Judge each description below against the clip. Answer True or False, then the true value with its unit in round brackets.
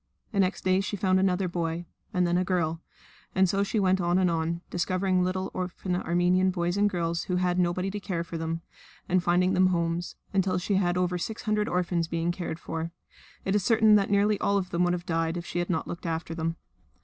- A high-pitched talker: False (180 Hz)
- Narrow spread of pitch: True (1.7 semitones)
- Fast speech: True (225 wpm)